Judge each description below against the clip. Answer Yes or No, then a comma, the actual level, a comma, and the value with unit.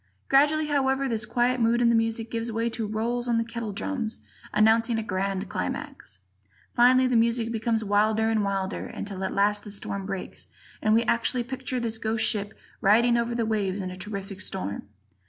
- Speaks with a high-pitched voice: Yes, high, 225 Hz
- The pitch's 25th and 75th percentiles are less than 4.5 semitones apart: Yes, narrow, 2.5 semitones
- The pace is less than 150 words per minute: No, average, 190 wpm